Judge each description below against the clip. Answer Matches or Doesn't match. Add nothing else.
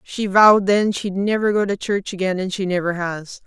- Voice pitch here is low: Doesn't match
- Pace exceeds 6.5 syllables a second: Doesn't match